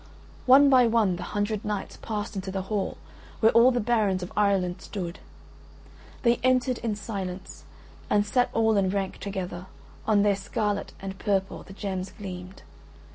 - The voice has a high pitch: Yes, high, 205 Hz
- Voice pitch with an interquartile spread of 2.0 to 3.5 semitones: Yes, average, 2.7 semitones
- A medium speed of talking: Yes, average, 160 wpm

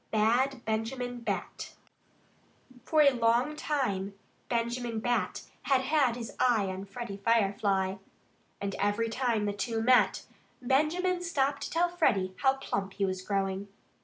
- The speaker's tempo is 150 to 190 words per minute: No, average, 140 wpm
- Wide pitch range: No, average, 4.9 semitones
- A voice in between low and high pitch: No, high, 235 Hz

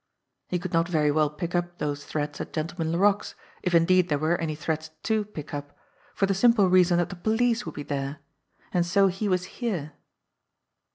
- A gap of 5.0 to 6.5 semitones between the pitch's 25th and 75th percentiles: No, average, 3.7 semitones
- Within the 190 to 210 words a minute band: Yes, average, 195 wpm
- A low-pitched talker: No, medium, 175 Hz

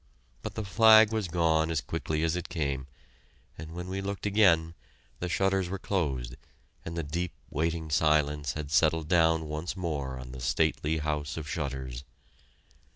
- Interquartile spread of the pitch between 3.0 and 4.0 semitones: Yes, average, 3.3 semitones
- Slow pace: No, average, 160 wpm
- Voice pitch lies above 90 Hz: No, very low, 80 Hz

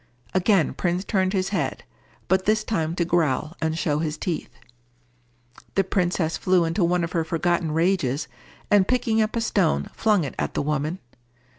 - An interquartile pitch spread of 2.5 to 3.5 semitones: Yes, average, 3.2 semitones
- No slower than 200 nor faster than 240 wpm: No, average, 170 wpm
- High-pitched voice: No, medium, 175 Hz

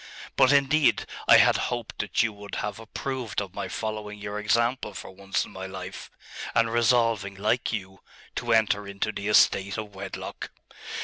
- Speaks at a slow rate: No, average, 170 wpm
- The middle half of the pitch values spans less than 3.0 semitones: Yes, narrow, 2.6 semitones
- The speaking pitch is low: Yes, low, 105 Hz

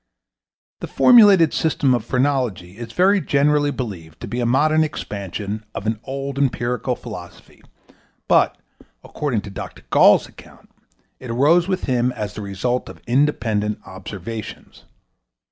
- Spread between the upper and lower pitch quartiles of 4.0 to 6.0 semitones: Yes, wide, 5.4 semitones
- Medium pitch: No, low, 125 Hz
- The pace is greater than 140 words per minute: No, slow, 135 wpm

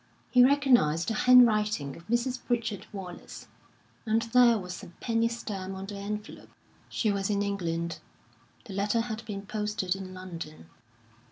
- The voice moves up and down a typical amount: Yes, average, 3.7 semitones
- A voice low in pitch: No, high, 210 Hz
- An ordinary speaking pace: Yes, average, 150 wpm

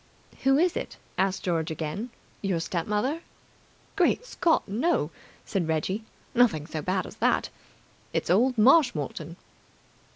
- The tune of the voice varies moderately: No, wide, 7.6 semitones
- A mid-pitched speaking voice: No, high, 195 Hz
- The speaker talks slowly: Yes, slow, 130 wpm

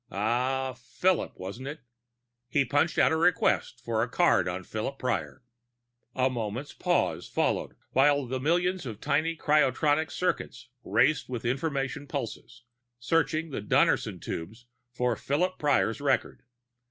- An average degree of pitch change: Yes, average, 4.1 semitones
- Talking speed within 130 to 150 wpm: Yes, slow, 135 wpm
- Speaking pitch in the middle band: No, low, 130 Hz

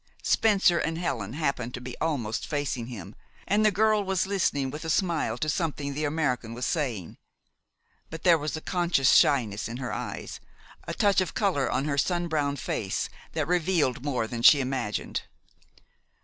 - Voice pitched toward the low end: No, medium, 145 Hz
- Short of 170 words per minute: No, average, 175 wpm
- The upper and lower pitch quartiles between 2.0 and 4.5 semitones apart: No, wide, 5.6 semitones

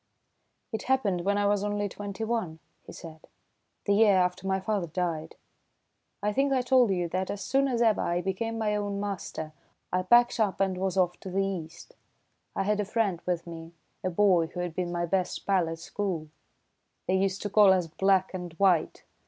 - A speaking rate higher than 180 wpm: Yes, average, 200 wpm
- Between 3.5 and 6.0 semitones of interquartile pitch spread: No, average, 2.7 semitones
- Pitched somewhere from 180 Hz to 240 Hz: Yes, high, 190 Hz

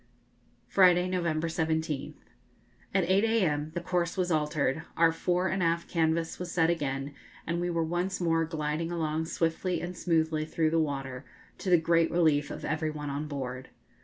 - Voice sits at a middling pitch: Yes, medium, 165 Hz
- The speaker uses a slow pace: No, average, 170 wpm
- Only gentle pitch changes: Yes, narrow, 2.3 semitones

